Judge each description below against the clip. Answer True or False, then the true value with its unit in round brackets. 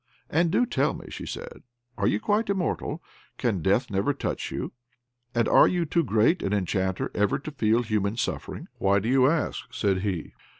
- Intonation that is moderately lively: False (7.8 semitones)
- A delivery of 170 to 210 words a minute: True (185 wpm)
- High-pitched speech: False (115 Hz)